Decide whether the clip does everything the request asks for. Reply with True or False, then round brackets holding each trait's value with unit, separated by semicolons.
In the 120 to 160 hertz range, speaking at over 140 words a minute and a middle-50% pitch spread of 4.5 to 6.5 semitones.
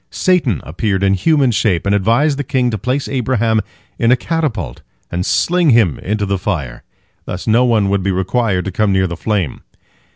False (110 Hz; 190 wpm; 4.8 semitones)